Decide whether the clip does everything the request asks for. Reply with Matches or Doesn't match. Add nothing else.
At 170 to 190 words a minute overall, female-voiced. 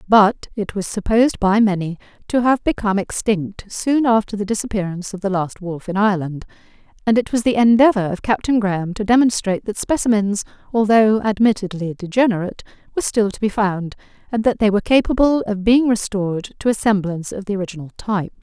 Matches